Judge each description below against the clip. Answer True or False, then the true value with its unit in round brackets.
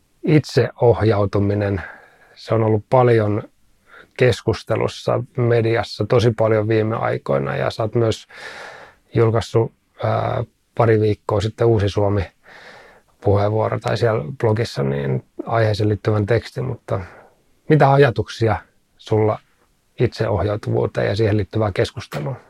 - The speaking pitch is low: True (110 Hz)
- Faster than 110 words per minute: False (100 wpm)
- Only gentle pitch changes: True (2.1 semitones)